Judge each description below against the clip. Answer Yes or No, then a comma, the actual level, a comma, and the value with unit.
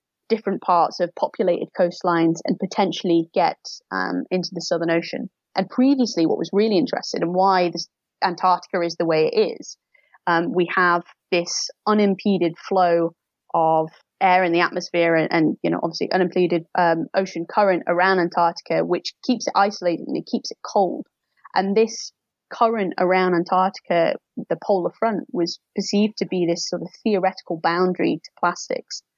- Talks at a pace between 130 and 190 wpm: Yes, average, 160 wpm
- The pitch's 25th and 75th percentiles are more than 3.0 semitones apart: No, narrow, 2.6 semitones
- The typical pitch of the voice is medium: Yes, medium, 180 Hz